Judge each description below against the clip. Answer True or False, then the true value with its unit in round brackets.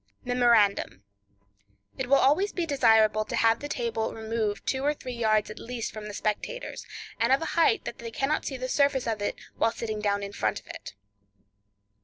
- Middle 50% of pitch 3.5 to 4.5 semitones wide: True (4.0 semitones)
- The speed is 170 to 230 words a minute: True (190 wpm)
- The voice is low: False (230 Hz)